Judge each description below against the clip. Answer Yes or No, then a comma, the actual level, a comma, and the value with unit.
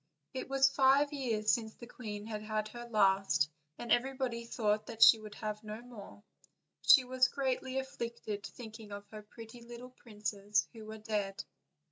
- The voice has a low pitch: No, high, 225 Hz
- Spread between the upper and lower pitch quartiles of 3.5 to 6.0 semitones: No, average, 2.8 semitones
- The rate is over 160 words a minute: Yes, average, 170 wpm